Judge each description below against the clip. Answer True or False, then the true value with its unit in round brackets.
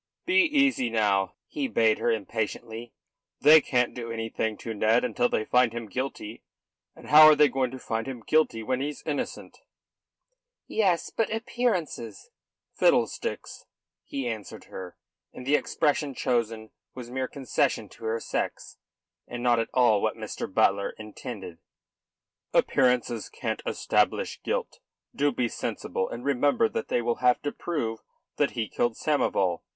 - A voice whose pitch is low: True (120 Hz)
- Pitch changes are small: False (4.3 semitones)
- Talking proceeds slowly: False (155 wpm)